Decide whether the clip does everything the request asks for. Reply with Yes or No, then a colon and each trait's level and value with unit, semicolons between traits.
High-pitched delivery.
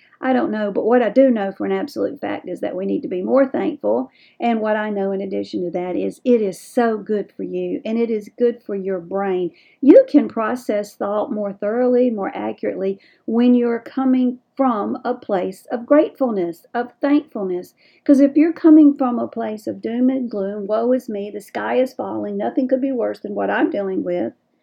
Yes: high, 230 Hz